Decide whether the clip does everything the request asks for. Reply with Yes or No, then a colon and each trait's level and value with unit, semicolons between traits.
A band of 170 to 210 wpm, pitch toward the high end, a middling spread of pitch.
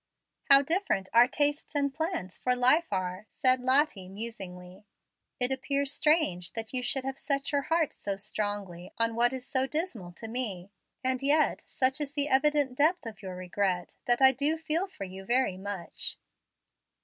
No: average, 175 wpm; very high, 255 Hz; wide, 6.3 semitones